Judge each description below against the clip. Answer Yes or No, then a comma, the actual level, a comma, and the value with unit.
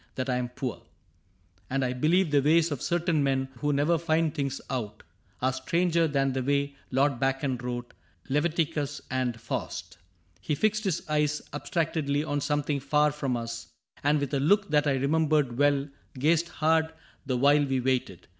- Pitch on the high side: No, medium, 145 Hz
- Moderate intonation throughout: Yes, average, 3.0 semitones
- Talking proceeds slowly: No, average, 175 wpm